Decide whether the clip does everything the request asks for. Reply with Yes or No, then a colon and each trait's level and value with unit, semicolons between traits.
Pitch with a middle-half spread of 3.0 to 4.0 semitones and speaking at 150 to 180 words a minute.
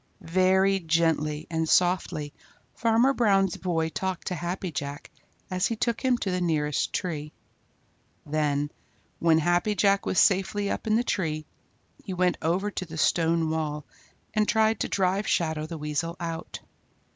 Yes: average, 3.6 semitones; average, 155 wpm